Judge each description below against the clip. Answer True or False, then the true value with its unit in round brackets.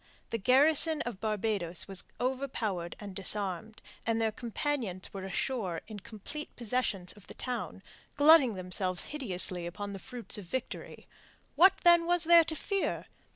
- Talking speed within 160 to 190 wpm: False (150 wpm)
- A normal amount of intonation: False (6.4 semitones)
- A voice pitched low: False (220 Hz)